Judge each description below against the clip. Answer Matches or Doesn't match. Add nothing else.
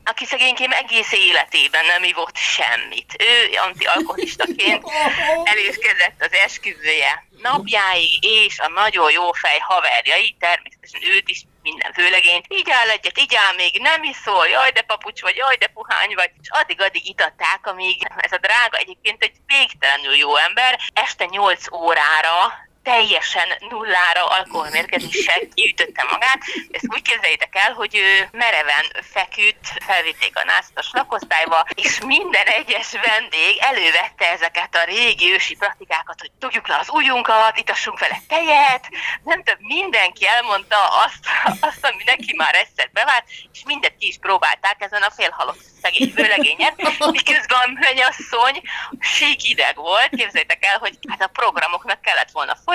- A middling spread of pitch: Doesn't match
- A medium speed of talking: Matches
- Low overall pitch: Doesn't match